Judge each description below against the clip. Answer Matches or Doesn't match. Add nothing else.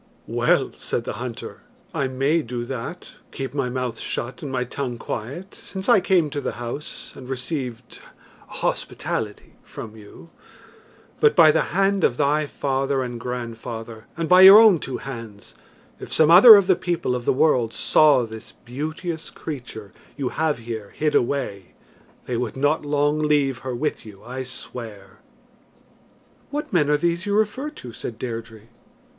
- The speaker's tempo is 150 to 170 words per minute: Matches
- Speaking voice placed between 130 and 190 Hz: Matches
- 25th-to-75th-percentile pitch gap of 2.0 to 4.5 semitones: Doesn't match